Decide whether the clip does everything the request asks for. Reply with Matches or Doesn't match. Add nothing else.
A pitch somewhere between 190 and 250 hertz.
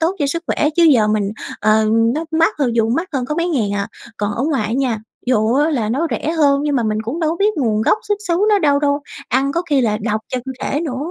Doesn't match